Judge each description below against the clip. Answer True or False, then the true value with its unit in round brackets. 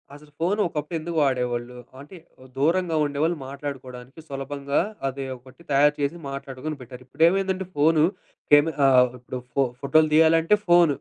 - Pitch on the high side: False (145 Hz)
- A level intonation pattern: False (3.3 semitones)